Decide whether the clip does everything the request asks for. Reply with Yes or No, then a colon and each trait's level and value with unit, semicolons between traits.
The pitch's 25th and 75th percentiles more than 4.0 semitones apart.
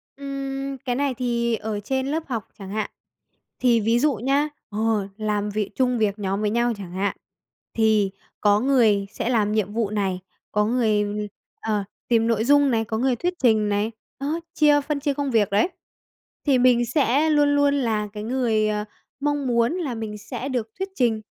Yes: average, 4.4 semitones